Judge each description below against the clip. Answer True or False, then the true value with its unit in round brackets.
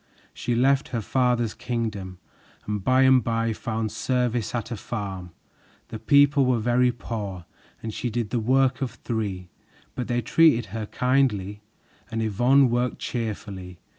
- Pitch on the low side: True (115 Hz)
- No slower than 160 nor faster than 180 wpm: False (150 wpm)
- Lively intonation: False (3.0 semitones)